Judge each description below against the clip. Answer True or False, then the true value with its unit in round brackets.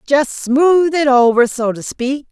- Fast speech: False (180 wpm)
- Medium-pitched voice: False (270 Hz)